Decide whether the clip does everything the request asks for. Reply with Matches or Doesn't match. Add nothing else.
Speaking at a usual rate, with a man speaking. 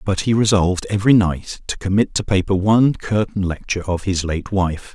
Matches